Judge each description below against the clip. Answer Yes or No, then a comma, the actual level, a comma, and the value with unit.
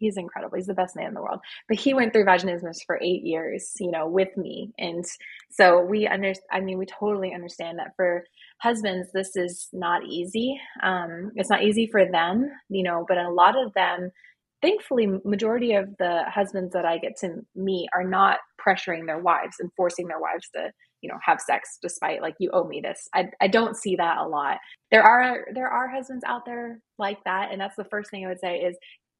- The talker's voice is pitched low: No, high, 190 Hz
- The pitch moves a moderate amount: Yes, average, 3.3 semitones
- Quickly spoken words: Yes, fast, 215 wpm